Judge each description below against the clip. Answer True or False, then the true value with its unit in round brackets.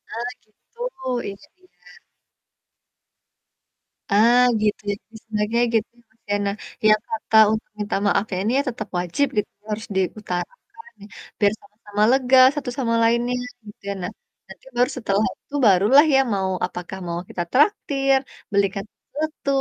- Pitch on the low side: False (220 Hz)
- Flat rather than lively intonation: False (4.3 semitones)